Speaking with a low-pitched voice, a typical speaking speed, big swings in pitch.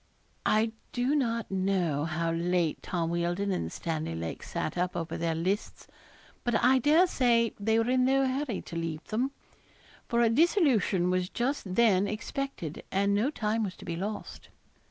No: high, 200 Hz; average, 170 wpm; wide, 5.9 semitones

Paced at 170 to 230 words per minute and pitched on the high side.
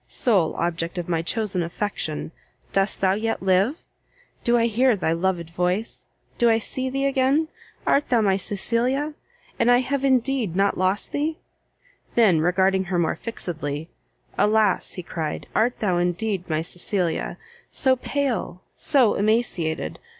No: average, 145 wpm; high, 205 Hz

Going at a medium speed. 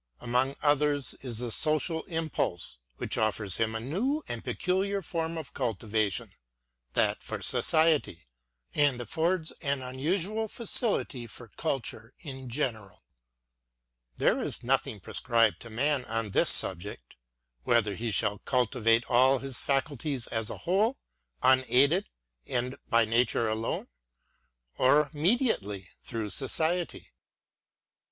No: slow, 130 wpm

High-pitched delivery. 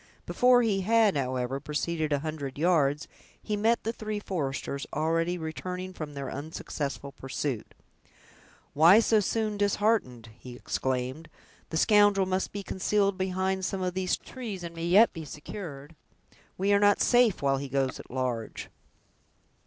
No: medium, 170 Hz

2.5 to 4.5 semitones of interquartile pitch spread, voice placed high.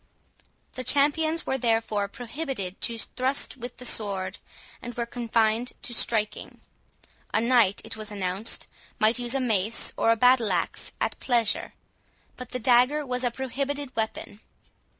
Yes: average, 2.8 semitones; high, 235 Hz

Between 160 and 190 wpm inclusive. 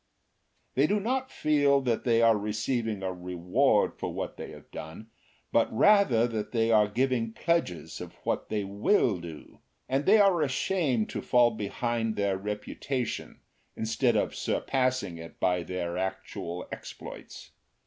No: average, 150 wpm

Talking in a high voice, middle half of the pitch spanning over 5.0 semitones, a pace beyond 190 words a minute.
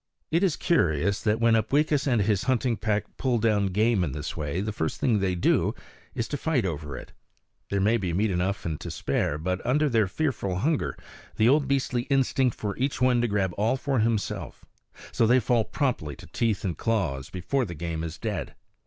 No: low, 110 Hz; wide, 5.5 semitones; fast, 205 wpm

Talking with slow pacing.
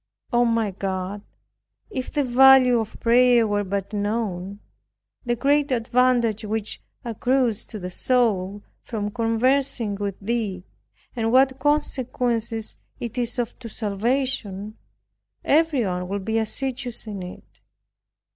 Yes: slow, 120 wpm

